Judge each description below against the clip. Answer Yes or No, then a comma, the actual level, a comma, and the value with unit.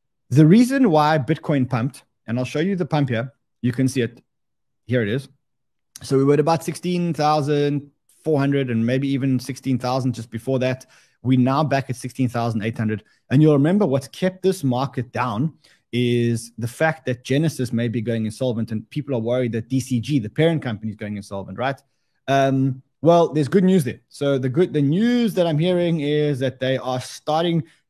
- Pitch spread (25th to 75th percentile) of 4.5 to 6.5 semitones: No, average, 3.6 semitones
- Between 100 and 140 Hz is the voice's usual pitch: Yes, low, 135 Hz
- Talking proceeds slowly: No, average, 200 wpm